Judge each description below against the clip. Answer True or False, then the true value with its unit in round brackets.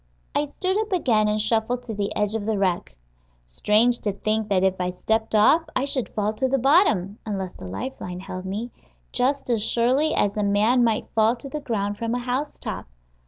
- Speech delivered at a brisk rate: True (210 wpm)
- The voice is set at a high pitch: True (220 Hz)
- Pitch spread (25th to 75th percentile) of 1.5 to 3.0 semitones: False (3.9 semitones)